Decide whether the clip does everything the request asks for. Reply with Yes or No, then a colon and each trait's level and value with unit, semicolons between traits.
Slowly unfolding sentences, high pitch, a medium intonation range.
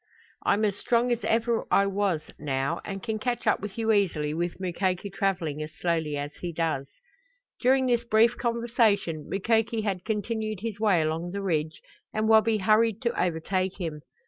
No: average, 170 wpm; high, 200 Hz; average, 4.8 semitones